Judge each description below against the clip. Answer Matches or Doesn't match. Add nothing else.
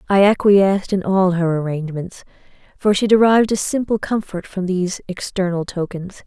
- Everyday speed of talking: Matches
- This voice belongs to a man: Doesn't match